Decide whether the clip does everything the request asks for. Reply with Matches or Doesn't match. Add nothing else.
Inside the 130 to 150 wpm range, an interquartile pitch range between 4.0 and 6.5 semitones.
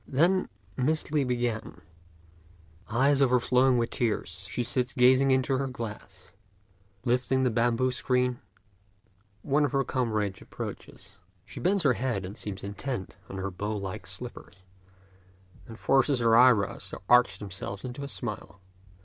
Doesn't match